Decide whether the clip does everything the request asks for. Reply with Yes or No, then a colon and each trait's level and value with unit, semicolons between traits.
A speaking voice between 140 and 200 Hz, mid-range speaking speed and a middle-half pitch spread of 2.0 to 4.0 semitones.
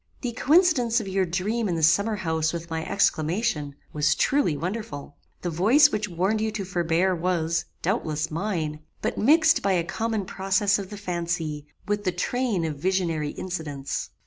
No: medium, 185 Hz; average, 170 wpm; average, 4.7 semitones